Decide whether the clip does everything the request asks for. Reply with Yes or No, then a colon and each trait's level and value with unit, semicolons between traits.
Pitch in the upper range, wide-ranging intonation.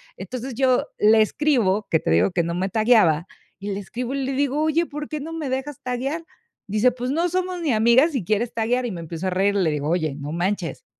Yes: high, 235 Hz; wide, 6.4 semitones